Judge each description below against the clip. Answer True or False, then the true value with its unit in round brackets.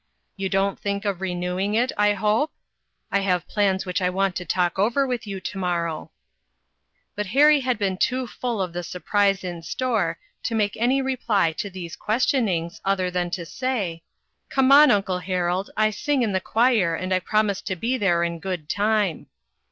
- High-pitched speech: True (195 Hz)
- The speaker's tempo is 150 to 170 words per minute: False (195 wpm)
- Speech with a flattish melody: False (3.6 semitones)